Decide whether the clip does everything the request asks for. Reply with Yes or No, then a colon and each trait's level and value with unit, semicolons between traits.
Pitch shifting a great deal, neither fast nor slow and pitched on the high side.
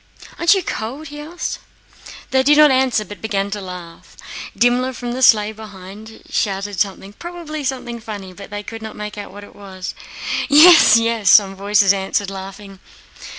No: average, 4.7 semitones; average, 160 wpm; high, 215 Hz